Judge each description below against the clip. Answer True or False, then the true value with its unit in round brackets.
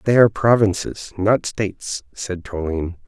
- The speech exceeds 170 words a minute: False (135 wpm)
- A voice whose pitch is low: True (100 Hz)